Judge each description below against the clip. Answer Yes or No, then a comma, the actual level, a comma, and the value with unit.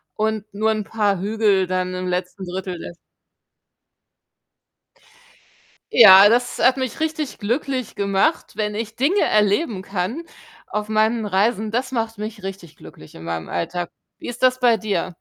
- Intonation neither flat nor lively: Yes, average, 3.6 semitones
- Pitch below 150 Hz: No, high, 210 Hz